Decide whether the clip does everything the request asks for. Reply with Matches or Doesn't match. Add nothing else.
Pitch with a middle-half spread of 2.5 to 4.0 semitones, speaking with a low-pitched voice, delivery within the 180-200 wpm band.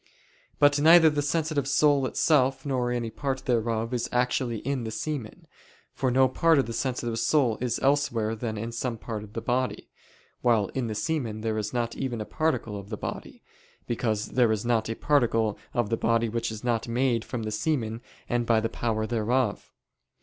Matches